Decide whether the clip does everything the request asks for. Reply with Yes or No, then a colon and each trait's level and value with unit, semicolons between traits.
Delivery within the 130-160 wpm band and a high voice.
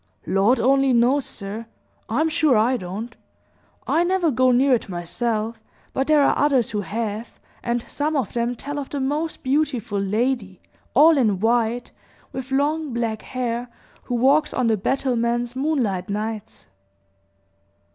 Yes: average, 145 wpm; high, 245 Hz